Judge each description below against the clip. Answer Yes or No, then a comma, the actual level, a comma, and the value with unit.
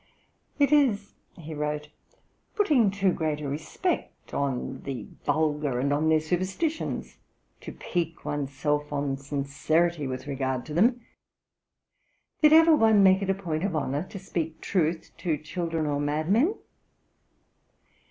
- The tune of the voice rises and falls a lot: No, average, 5.0 semitones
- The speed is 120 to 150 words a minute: Yes, average, 140 wpm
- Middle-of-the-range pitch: Yes, medium, 160 Hz